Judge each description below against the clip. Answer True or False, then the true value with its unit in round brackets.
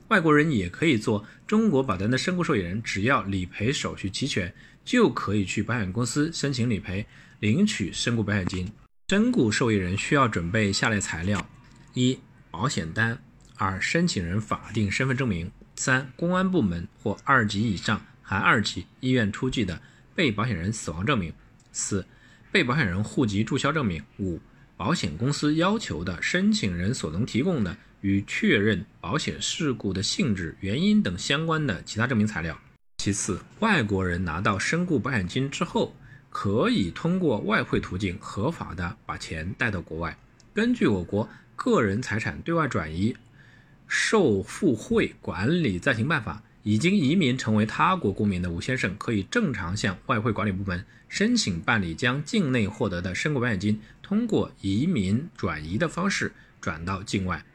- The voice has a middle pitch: False (110 Hz)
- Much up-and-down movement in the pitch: False (5.0 semitones)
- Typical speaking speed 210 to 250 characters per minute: False (260 characters per minute)